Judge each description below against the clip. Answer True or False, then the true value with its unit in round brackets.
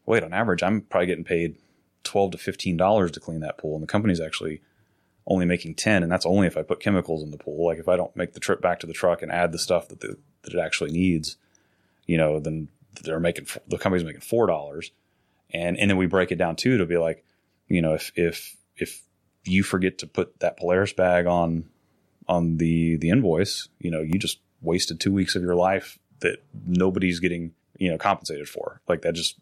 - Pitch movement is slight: True (2.2 semitones)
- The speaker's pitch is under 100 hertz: True (85 Hz)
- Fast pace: True (225 wpm)